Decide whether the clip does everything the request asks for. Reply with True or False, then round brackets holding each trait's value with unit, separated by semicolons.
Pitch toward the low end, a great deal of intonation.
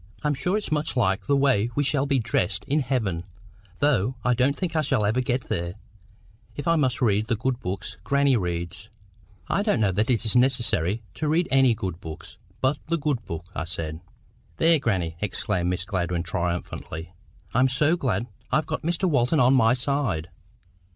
True (120 Hz; 7.1 semitones)